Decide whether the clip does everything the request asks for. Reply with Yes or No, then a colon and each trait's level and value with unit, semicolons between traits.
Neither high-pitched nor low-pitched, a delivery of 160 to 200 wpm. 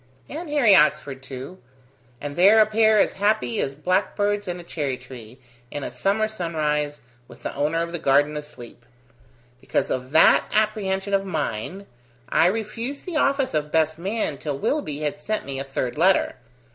Yes: medium, 170 Hz; average, 170 wpm